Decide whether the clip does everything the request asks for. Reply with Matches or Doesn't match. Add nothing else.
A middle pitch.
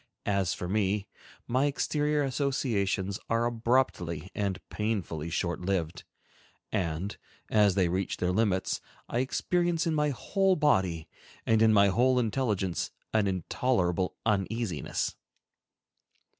Doesn't match